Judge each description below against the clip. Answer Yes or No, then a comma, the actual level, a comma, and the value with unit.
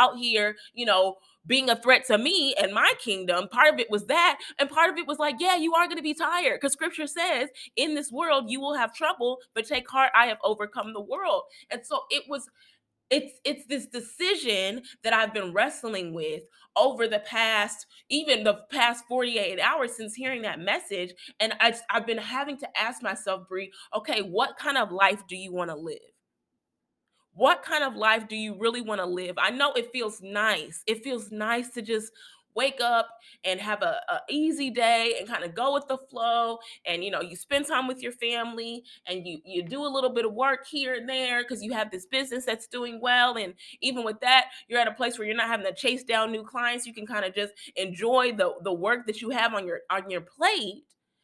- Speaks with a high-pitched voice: Yes, high, 235 Hz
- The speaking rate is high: Yes, fast, 225 wpm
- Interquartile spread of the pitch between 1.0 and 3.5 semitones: No, average, 4.1 semitones